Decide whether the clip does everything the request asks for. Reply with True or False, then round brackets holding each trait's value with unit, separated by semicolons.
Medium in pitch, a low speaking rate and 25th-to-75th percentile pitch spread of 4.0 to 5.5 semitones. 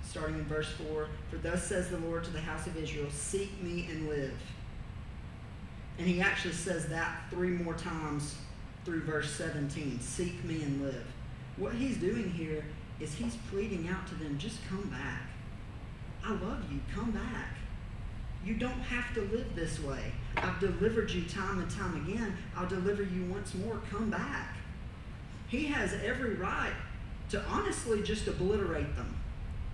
False (165 Hz; 165 wpm; 5.2 semitones)